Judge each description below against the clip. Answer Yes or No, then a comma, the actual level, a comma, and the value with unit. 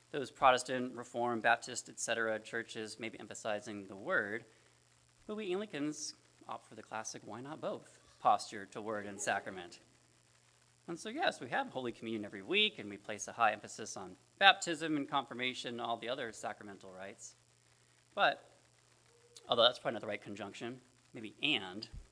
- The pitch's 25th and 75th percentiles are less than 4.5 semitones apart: Yes, average, 4.1 semitones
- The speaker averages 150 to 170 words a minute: Yes, average, 165 wpm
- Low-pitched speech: Yes, low, 115 Hz